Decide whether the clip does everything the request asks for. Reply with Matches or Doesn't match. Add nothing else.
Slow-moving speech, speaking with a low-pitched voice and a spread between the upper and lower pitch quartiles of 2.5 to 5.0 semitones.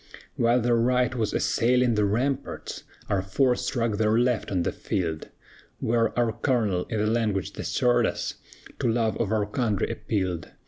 Doesn't match